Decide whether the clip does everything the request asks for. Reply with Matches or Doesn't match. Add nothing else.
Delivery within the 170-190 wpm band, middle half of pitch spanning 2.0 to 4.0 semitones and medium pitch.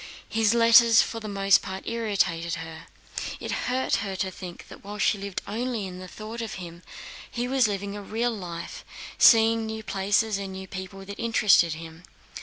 Doesn't match